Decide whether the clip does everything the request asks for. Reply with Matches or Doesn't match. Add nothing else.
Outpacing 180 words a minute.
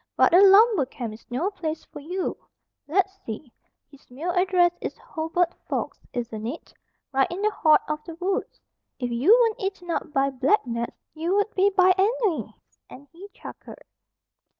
Doesn't match